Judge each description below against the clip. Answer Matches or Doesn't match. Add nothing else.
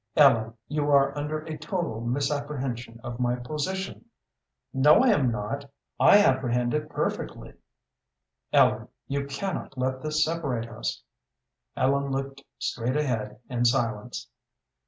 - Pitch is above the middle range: Doesn't match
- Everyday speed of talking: Doesn't match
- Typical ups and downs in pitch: Matches